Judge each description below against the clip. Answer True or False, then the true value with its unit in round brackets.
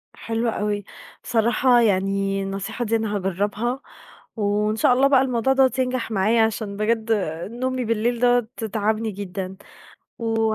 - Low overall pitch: False (220 Hz)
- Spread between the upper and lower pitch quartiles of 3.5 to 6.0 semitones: False (2.9 semitones)